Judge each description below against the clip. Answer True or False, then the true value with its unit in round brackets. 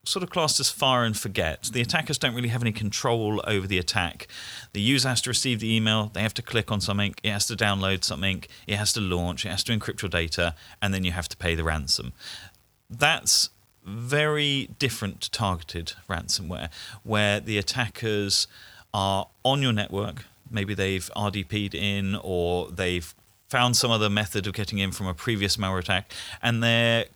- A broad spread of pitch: False (3.4 semitones)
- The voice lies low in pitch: True (105 Hz)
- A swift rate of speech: False (190 wpm)